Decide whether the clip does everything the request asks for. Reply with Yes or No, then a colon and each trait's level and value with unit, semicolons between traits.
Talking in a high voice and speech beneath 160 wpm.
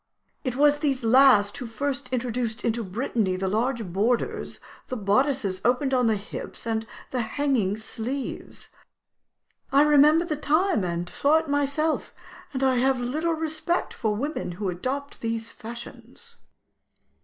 Yes: very high, 250 Hz; average, 145 wpm